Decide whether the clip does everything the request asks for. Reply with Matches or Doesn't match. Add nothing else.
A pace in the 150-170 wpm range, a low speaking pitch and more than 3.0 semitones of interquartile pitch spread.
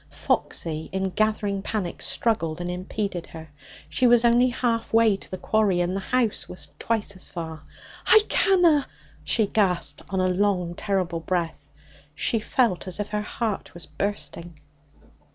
Doesn't match